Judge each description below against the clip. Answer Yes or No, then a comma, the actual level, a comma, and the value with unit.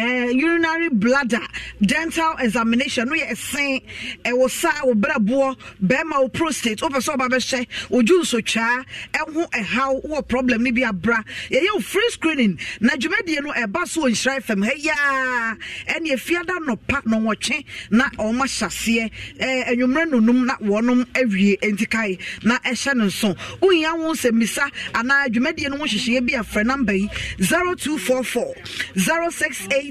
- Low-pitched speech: No, very high, 255 Hz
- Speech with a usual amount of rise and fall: Yes, average, 3.9 semitones